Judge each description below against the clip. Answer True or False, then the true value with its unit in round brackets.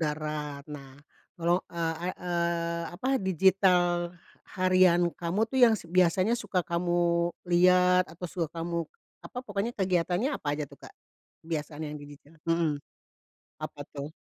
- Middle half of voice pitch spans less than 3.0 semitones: True (2.4 semitones)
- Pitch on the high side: False (170 Hz)